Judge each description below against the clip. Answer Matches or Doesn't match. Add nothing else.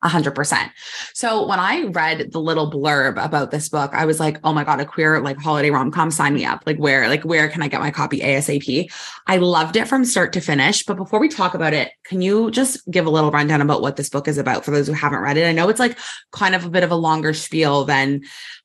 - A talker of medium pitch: Matches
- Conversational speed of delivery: Doesn't match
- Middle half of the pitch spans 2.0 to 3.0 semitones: Doesn't match